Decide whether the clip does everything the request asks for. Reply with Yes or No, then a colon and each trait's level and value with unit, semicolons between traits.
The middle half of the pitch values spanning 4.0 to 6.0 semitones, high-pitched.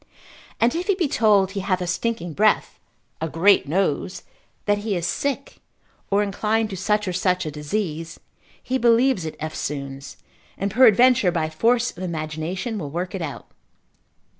Yes: average, 5.2 semitones; high, 195 Hz